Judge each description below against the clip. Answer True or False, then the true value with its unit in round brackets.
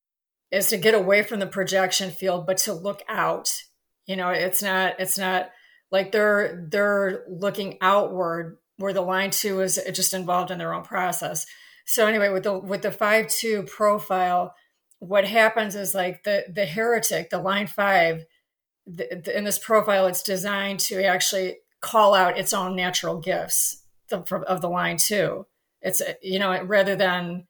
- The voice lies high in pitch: True (195 Hz)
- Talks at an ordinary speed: True (170 wpm)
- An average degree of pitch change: False (1.8 semitones)